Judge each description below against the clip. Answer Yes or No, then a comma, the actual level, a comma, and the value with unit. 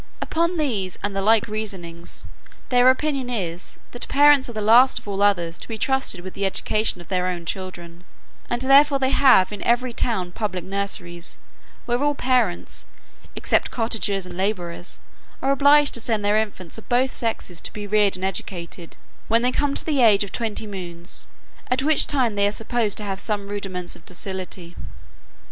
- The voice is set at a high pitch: Yes, high, 210 Hz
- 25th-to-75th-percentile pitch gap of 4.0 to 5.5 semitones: Yes, average, 5.1 semitones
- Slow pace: No, average, 185 wpm